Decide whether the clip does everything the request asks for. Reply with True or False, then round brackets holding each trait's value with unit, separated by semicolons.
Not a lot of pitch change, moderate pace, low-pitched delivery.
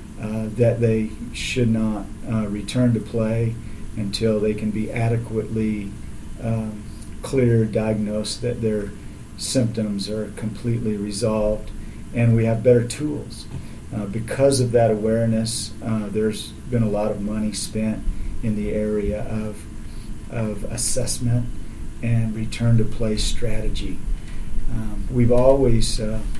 False (1.5 semitones; 125 wpm; 110 Hz)